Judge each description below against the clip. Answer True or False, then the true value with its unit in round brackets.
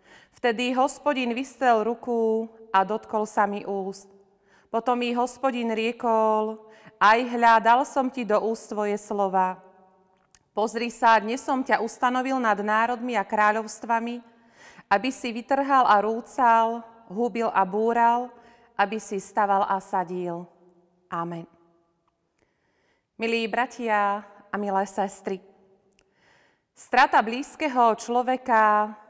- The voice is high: True (220 Hz)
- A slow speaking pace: True (105 wpm)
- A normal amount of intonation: True (3.1 semitones)